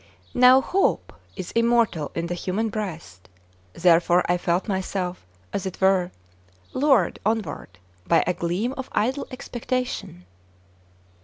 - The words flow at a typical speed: No, slow, 125 wpm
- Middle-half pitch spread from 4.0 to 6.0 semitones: Yes, average, 5.3 semitones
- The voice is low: No, high, 190 Hz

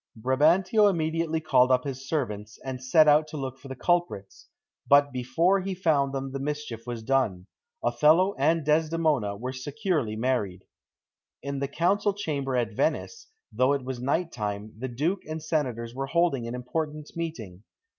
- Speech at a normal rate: Yes, average, 165 wpm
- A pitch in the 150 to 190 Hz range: No, medium, 140 Hz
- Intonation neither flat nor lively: Yes, average, 4.4 semitones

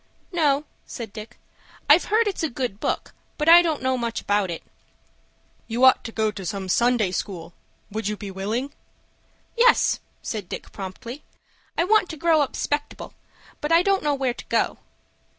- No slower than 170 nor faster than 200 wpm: Yes, average, 175 wpm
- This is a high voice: Yes, very high, 250 Hz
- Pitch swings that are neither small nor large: No, wide, 6.9 semitones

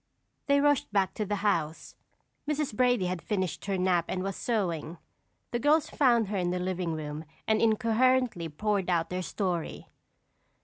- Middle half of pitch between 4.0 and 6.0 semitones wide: Yes, average, 4.8 semitones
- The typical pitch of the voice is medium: No, high, 195 Hz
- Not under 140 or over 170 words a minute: Yes, average, 165 wpm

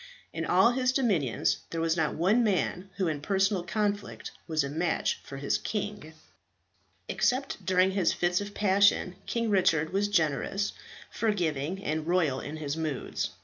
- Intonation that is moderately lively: Yes, average, 4.5 semitones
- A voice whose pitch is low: No, medium, 180 Hz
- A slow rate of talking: No, average, 155 wpm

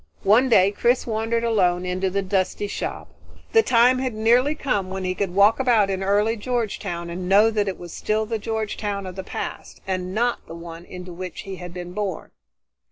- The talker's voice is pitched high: Yes, high, 200 Hz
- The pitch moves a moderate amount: Yes, average, 3.5 semitones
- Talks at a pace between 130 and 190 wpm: No, fast, 205 wpm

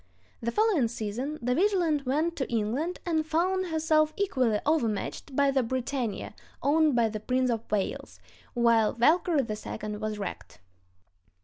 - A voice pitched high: Yes, very high, 265 Hz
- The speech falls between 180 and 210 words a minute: No, average, 140 wpm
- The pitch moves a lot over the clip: Yes, wide, 5.8 semitones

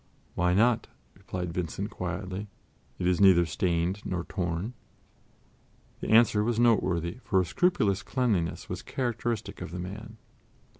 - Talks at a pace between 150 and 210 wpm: No, slow, 135 wpm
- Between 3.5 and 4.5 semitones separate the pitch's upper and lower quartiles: Yes, average, 3.9 semitones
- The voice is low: Yes, very low, 95 Hz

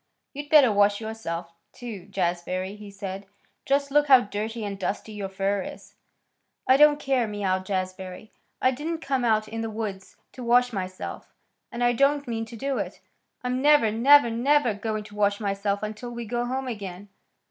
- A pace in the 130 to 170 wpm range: No, average, 180 wpm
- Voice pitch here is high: Yes, high, 220 Hz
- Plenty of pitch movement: No, average, 4.0 semitones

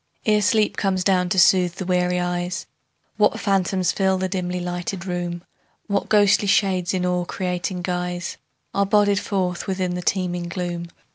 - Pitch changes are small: Yes, narrow, 1.5 semitones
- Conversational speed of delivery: Yes, average, 160 wpm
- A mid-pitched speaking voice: Yes, medium, 180 Hz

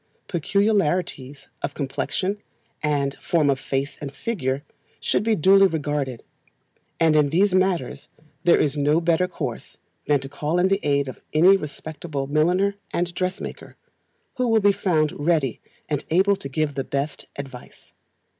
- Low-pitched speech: No, medium, 155 Hz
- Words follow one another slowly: No, average, 150 wpm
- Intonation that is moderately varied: Yes, average, 4.7 semitones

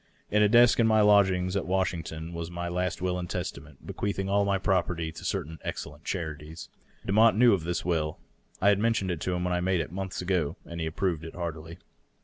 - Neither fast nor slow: No, fast, 230 wpm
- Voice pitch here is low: Yes, very low, 90 Hz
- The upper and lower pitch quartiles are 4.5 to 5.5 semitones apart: No, average, 2.9 semitones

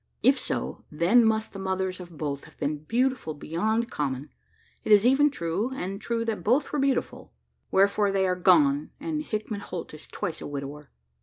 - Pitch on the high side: Yes, high, 195 Hz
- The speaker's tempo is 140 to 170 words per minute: No, average, 185 wpm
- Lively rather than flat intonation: Yes, wide, 6.8 semitones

